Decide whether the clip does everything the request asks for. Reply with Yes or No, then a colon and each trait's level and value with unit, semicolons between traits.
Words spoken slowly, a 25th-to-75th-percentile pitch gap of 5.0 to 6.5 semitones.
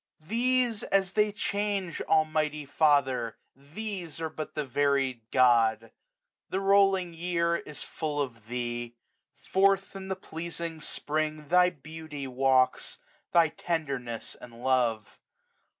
Yes: slow, 120 wpm; wide, 5.6 semitones